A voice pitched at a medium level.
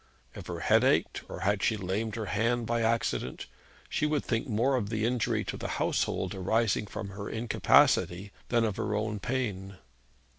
No: low, 110 Hz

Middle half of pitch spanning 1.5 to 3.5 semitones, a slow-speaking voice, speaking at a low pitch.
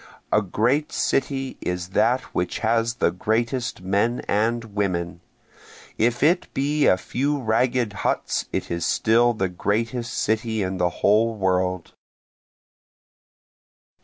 No: average, 4.2 semitones; slow, 125 wpm; low, 110 Hz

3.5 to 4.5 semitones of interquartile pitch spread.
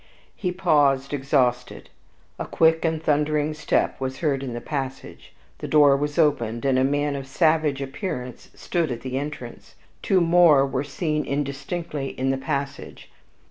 No: narrow, 2.5 semitones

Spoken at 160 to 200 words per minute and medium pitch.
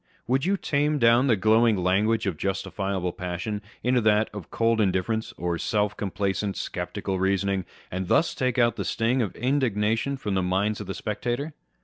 No: average, 170 wpm; low, 105 Hz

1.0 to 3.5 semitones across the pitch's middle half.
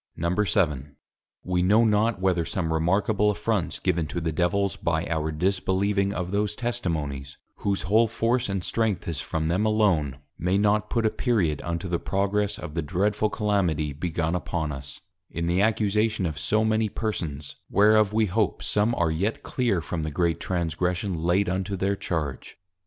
No: average, 4.2 semitones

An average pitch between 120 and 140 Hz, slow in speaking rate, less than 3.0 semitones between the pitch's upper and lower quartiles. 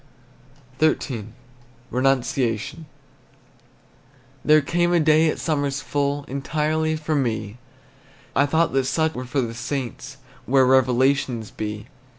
No: low, 135 Hz; slow, 115 wpm; average, 3.6 semitones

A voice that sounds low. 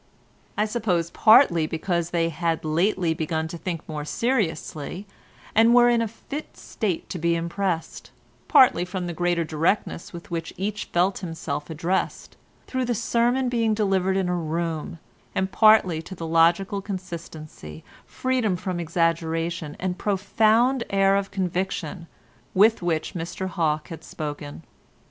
No: medium, 175 Hz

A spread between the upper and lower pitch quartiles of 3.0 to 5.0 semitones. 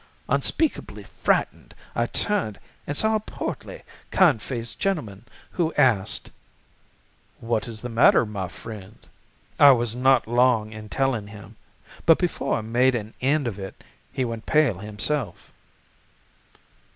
Yes: average, 4.2 semitones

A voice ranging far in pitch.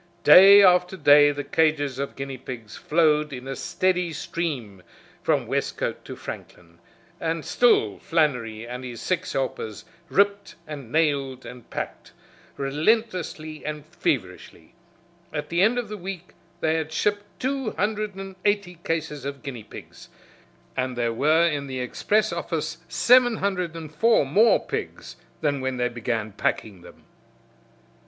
Yes: wide, 6.0 semitones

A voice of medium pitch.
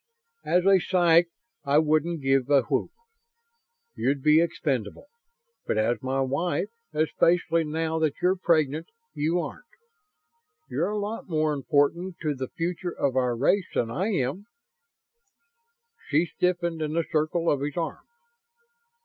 Yes: medium, 155 Hz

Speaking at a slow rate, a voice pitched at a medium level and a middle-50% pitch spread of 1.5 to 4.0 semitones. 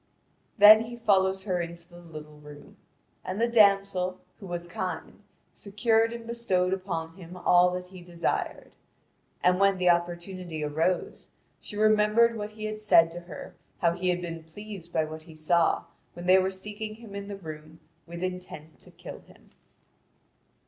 No: average, 165 wpm; medium, 180 Hz; average, 3.3 semitones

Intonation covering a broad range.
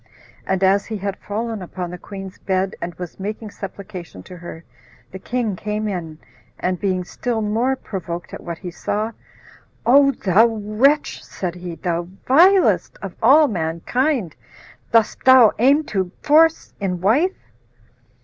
No: average, 4.5 semitones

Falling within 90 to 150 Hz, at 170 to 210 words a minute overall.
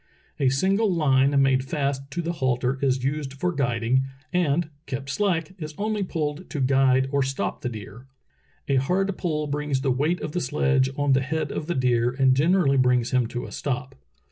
Yes: medium, 140 Hz; average, 195 wpm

